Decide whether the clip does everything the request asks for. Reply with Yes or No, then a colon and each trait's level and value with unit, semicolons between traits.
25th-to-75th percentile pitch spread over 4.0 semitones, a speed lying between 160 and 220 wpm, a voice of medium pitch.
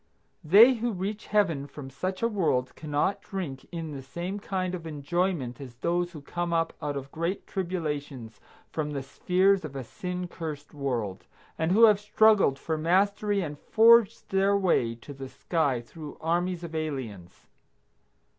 Yes: average, 5.2 semitones; average, 165 wpm; medium, 165 Hz